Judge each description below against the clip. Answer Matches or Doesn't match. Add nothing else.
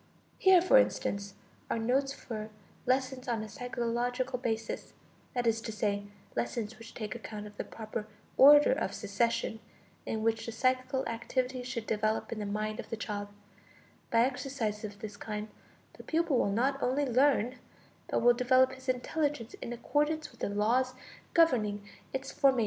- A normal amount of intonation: Matches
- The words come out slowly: Doesn't match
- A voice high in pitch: Matches